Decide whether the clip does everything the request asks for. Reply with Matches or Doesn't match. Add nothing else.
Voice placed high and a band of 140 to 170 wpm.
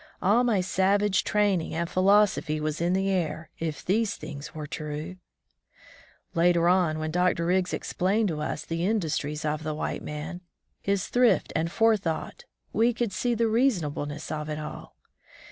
Doesn't match